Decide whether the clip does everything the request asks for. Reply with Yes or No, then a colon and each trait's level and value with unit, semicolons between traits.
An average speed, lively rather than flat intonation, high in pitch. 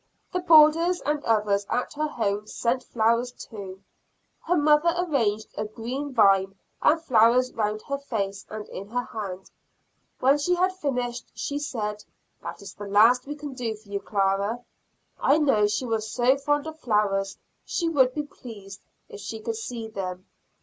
Yes: average, 170 wpm; wide, 5.7 semitones; high, 235 Hz